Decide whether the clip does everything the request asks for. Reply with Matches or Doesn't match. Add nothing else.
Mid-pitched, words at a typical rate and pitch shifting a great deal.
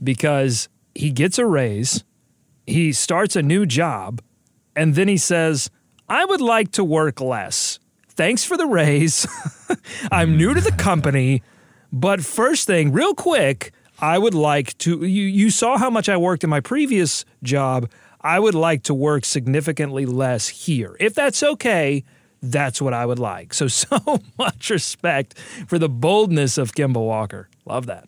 Matches